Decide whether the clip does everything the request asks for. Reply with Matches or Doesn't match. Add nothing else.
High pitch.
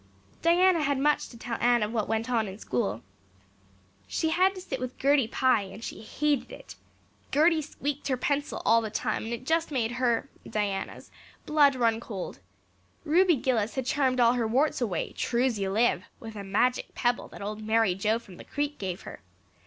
Matches